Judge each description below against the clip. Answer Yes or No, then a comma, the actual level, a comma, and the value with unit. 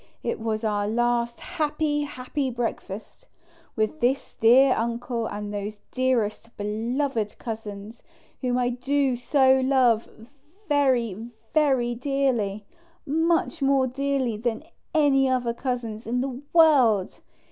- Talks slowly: Yes, slow, 115 wpm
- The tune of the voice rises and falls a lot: No, average, 3.4 semitones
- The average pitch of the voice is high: Yes, high, 245 Hz